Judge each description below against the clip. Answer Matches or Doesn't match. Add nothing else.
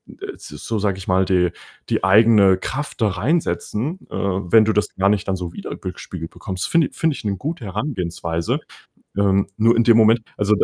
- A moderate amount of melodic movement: Matches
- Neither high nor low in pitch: Doesn't match